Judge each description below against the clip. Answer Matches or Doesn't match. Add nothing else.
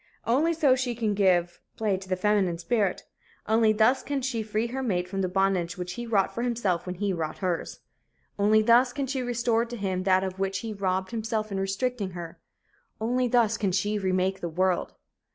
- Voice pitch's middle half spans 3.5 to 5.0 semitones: Matches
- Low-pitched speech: Doesn't match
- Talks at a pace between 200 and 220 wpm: Matches